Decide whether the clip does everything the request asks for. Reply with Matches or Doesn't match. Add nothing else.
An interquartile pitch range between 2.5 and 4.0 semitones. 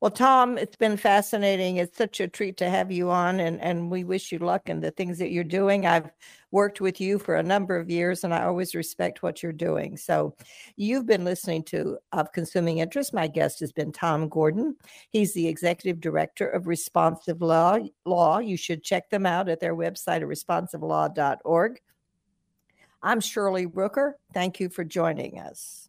Matches